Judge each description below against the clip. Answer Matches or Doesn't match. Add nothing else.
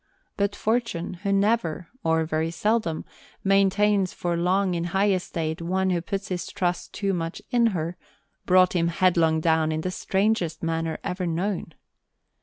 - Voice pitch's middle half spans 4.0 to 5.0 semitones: Doesn't match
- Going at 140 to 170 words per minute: Matches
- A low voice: Doesn't match